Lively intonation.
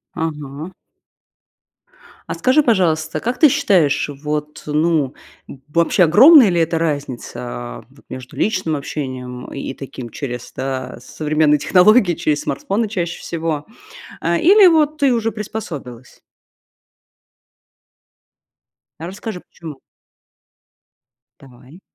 Yes: wide, 6.1 semitones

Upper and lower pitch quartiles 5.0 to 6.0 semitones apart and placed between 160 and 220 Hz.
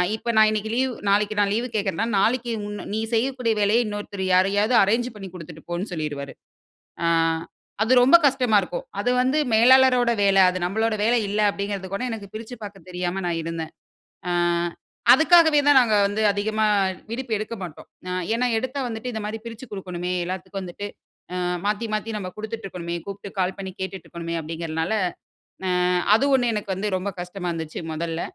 No: average, 4.0 semitones; high, 205 Hz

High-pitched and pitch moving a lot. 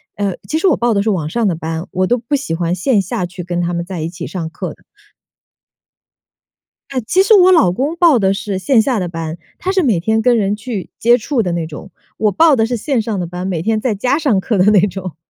Yes: high, 205 Hz; wide, 5.7 semitones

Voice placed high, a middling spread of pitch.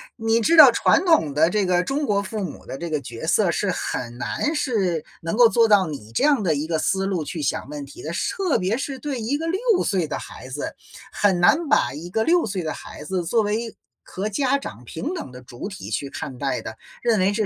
No: high, 195 Hz; wide, 7.6 semitones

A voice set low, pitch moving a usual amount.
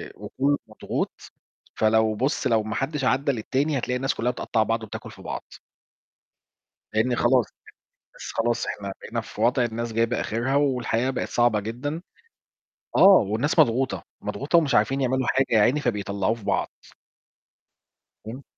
Yes: low, 120 Hz; average, 3.3 semitones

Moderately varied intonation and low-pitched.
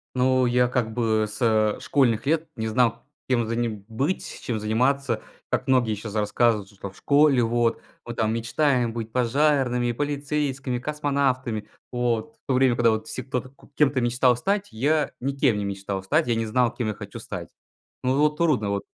Yes: average, 3.6 semitones; low, 120 Hz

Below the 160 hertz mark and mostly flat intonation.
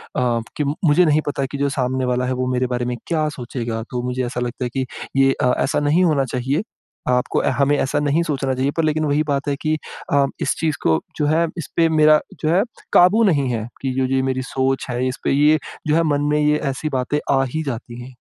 No: medium, 140 Hz; average, 3.1 semitones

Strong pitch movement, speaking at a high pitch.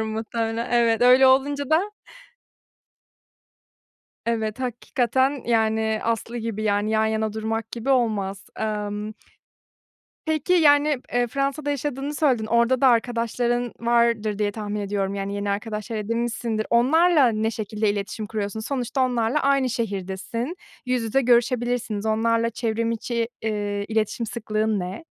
No: narrow, 2.5 semitones; high, 230 Hz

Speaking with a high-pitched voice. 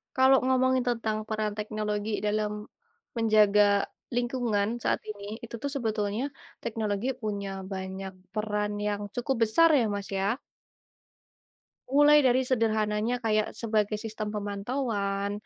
Yes: high, 215 Hz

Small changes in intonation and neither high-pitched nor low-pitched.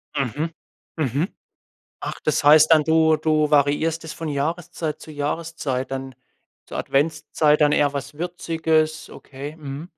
Yes: narrow, 1.9 semitones; medium, 155 Hz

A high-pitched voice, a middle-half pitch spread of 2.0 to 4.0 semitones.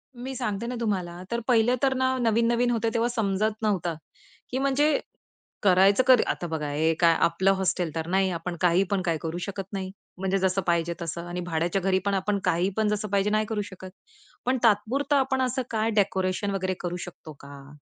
No: high, 195 Hz; average, 4.6 semitones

